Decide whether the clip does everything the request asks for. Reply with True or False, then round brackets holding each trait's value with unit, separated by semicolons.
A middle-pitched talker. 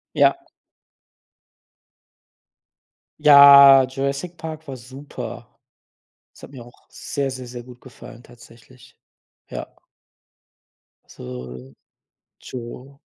False (130 Hz)